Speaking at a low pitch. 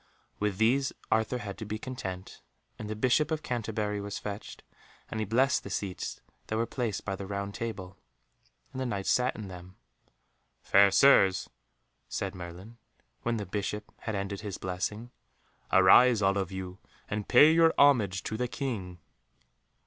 Yes: low, 105 Hz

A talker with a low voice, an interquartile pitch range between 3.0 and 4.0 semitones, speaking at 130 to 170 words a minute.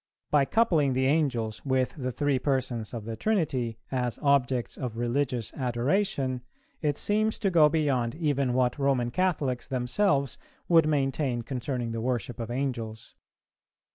Yes: low, 130 Hz; average, 3.3 semitones; average, 140 wpm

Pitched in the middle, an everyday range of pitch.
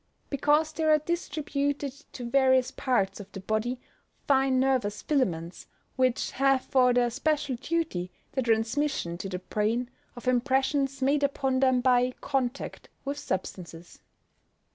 No: very high, 260 Hz; average, 3.0 semitones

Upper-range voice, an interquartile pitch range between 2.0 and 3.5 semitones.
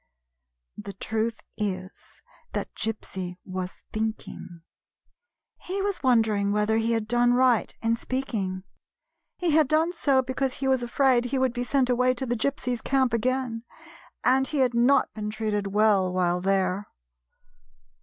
No: high, 235 Hz; average, 3.9 semitones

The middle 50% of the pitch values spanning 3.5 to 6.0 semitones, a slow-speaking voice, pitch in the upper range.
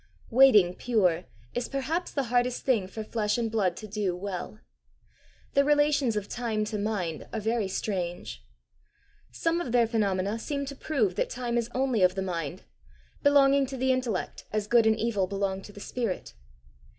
No: average, 4.7 semitones; average, 175 wpm; high, 220 Hz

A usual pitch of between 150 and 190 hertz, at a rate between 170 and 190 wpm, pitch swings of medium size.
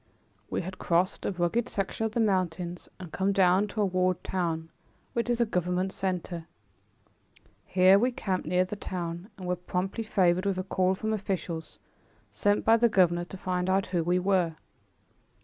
No: medium, 185 Hz; average, 180 wpm; narrow, 2.0 semitones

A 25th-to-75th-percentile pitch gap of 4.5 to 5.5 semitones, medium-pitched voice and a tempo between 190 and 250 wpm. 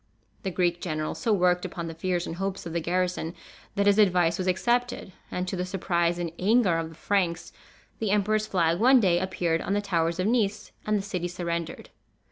No: average, 2.8 semitones; medium, 180 Hz; fast, 205 wpm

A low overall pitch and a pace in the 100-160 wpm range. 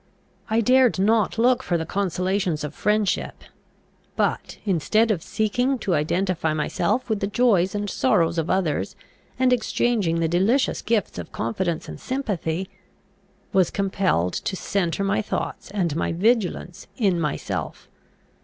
No: high, 195 Hz; average, 140 wpm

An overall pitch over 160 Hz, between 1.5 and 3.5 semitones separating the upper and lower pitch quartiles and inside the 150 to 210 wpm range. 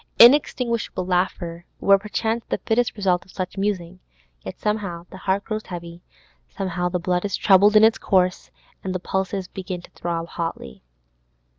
Yes: high, 190 Hz; average, 2.9 semitones; average, 160 wpm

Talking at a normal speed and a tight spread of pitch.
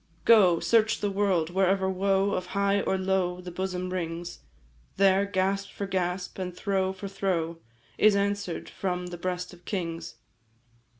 Yes: average, 155 wpm; narrow, 1.8 semitones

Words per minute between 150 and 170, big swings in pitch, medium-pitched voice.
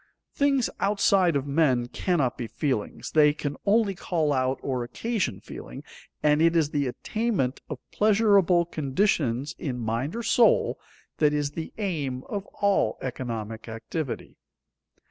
No: average, 140 wpm; wide, 7.2 semitones; medium, 150 Hz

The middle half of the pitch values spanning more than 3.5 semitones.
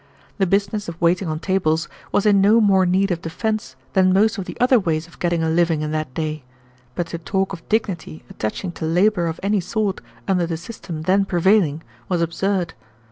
No: average, 3.2 semitones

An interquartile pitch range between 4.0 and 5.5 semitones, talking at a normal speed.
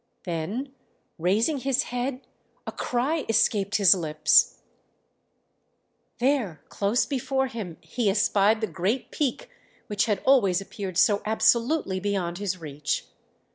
No: average, 5.0 semitones; slow, 120 wpm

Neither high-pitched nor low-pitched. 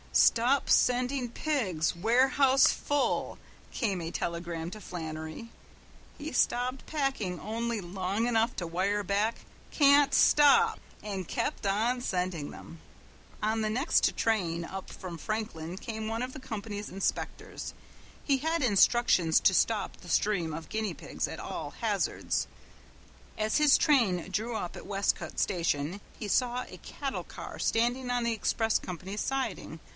No: high, 215 Hz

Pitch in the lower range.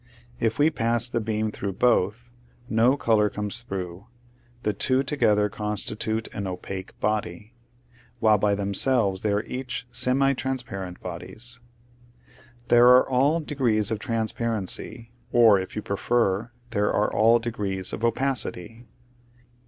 Yes: low, 110 Hz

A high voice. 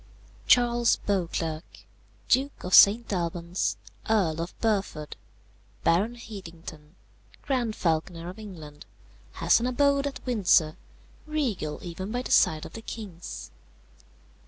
Yes: high, 195 Hz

